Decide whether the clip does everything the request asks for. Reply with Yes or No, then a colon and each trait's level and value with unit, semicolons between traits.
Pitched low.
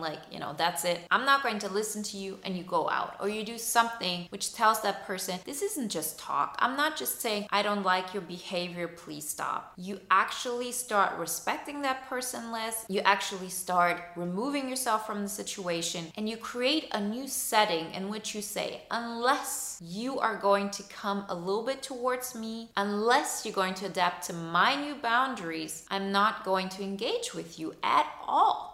No: high, 200 Hz